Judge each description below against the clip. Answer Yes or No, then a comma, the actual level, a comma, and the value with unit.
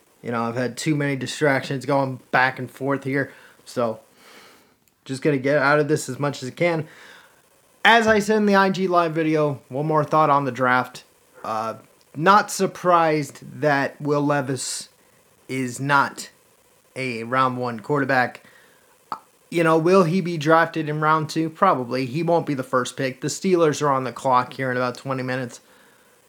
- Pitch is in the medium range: Yes, medium, 145 Hz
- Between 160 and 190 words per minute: Yes, average, 180 wpm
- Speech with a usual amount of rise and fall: Yes, average, 4.6 semitones